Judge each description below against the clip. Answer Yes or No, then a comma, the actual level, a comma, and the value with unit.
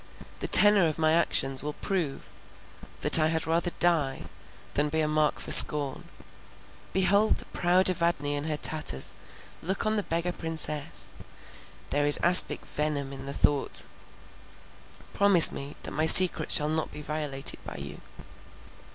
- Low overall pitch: No, medium, 155 Hz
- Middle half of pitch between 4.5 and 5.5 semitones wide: No, average, 3.0 semitones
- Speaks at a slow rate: No, average, 145 wpm